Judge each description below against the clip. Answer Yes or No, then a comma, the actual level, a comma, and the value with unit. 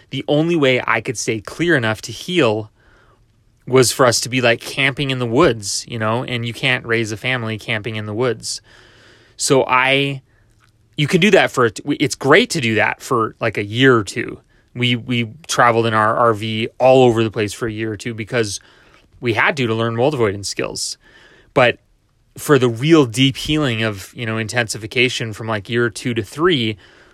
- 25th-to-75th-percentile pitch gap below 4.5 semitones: Yes, average, 2.7 semitones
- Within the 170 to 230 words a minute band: Yes, average, 200 wpm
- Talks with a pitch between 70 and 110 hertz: No, low, 120 Hz